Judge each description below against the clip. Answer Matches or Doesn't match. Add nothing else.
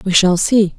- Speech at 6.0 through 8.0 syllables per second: Doesn't match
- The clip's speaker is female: Matches